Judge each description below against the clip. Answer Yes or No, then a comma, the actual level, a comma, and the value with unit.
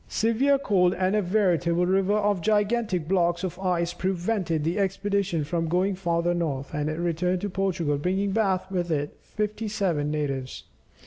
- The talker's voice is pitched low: No, medium, 180 Hz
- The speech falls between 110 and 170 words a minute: Yes, average, 165 wpm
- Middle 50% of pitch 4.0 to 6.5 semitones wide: No, average, 3.0 semitones